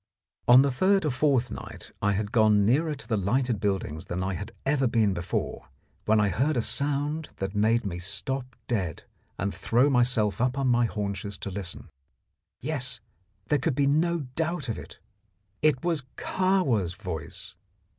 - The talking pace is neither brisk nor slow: Yes, average, 170 wpm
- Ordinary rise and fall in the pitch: No, wide, 5.7 semitones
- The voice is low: Yes, low, 120 Hz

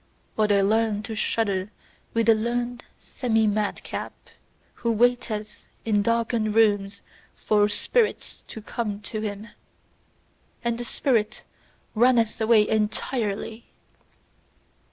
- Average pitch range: No, narrow, 1.9 semitones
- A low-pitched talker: No, high, 220 Hz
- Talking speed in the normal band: No, slow, 110 wpm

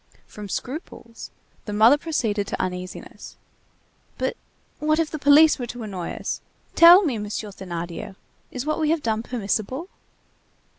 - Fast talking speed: No, average, 145 wpm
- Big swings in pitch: Yes, wide, 6.9 semitones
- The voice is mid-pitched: No, high, 235 Hz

